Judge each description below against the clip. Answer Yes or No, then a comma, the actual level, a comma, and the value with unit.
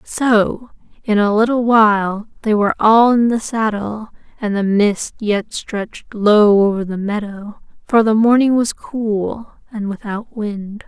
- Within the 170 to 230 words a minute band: No, average, 155 wpm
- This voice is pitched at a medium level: No, high, 215 Hz